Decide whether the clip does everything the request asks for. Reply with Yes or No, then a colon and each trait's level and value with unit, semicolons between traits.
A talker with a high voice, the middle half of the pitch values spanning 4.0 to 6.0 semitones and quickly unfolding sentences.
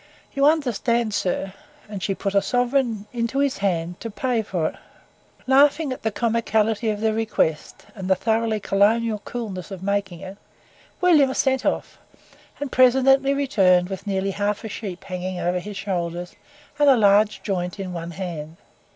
No: high, 210 Hz; average, 4.4 semitones; average, 160 wpm